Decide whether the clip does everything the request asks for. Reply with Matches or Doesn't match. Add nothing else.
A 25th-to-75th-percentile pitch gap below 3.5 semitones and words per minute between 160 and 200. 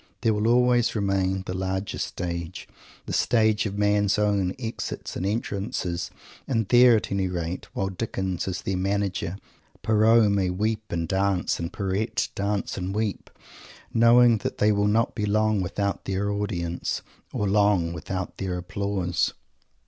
Doesn't match